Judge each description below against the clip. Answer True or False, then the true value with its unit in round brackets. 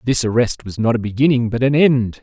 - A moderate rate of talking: False (240 wpm)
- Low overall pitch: True (120 Hz)